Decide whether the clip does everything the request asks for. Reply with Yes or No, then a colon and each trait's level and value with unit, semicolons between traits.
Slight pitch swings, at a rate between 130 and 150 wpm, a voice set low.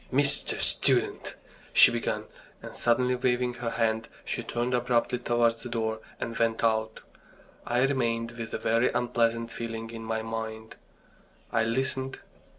Yes: narrow, 1.4 semitones; average, 145 wpm; low, 115 Hz